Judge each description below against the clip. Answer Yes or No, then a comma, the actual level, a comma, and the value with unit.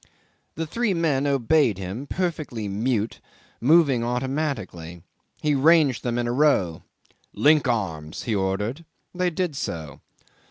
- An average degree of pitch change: No, wide, 7.0 semitones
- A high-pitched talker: No, low, 130 Hz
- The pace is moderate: No, slow, 125 wpm